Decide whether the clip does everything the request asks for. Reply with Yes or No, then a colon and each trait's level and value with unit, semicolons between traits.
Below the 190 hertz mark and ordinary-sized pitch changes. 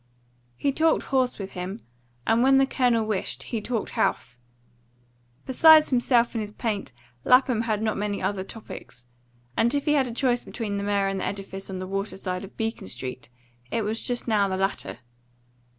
No: high, 215 Hz; average, 4.0 semitones